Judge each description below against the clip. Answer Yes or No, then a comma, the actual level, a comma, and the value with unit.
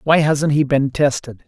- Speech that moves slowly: No, fast, 205 wpm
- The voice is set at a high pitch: No, medium, 145 Hz